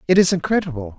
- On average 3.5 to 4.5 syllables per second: No, 7.2 syllables/s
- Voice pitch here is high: No, medium, 160 Hz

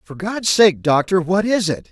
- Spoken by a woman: No, male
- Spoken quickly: Yes, fast, 220 wpm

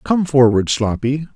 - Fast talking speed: No, slow, 135 wpm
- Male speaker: Yes, male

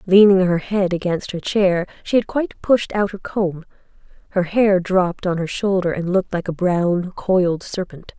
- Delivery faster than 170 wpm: Yes, average, 190 wpm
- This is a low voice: No, medium, 185 Hz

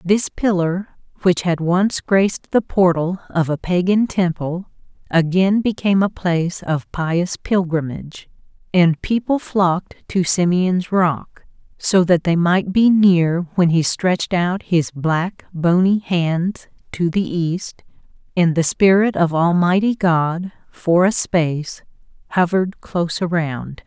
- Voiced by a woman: Yes, female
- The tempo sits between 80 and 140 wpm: Yes, slow, 135 wpm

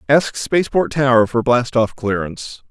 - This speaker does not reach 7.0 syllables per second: Yes, 5.0 syllables/s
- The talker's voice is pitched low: Yes, low, 125 Hz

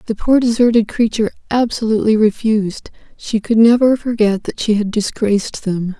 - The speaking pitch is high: Yes, high, 220 Hz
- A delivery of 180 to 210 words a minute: No, average, 150 wpm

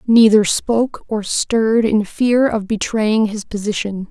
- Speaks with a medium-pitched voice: No, high, 215 Hz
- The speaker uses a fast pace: No, average, 145 wpm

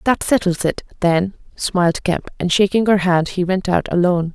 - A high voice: No, medium, 180 Hz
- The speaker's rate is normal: Yes, average, 195 wpm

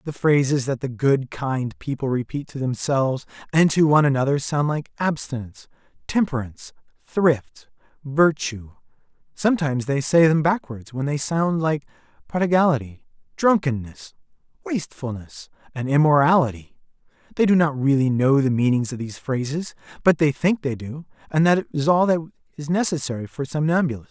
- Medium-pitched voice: Yes, medium, 145 Hz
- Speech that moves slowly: No, average, 145 wpm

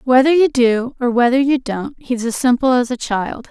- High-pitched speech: Yes, very high, 250 Hz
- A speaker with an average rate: No, fast, 220 wpm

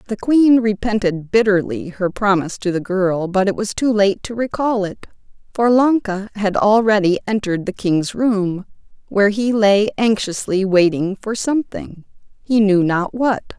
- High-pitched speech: Yes, high, 205 Hz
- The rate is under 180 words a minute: Yes, average, 160 wpm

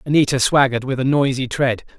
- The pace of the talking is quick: No, average, 180 wpm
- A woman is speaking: No, male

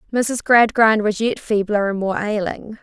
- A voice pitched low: No, high, 215 Hz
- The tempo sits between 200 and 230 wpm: No, average, 170 wpm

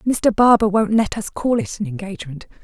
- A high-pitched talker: Yes, high, 225 Hz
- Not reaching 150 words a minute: No, fast, 205 wpm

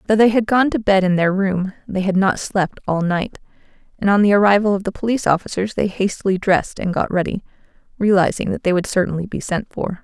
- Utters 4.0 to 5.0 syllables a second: No, 6.0 syllables/s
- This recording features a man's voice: No, female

